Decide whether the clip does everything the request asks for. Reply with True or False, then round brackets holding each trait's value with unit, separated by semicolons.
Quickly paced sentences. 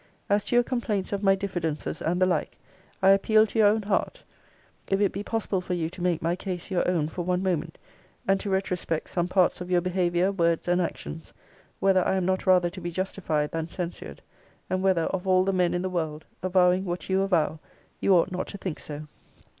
True (215 wpm)